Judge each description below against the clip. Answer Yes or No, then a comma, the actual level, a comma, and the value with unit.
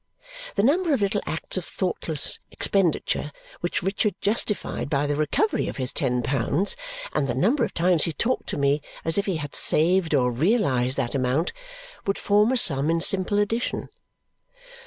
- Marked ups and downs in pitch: Yes, wide, 6.4 semitones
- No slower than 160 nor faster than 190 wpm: Yes, average, 175 wpm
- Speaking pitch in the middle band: Yes, medium, 170 Hz